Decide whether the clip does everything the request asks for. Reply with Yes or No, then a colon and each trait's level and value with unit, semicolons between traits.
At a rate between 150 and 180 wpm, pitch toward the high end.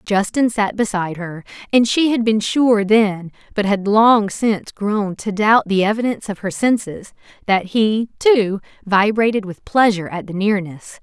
Yes: average, 170 wpm; high, 210 Hz